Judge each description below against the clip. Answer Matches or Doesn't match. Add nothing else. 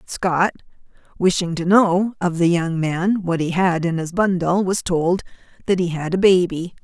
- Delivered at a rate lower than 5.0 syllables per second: Matches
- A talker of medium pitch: Matches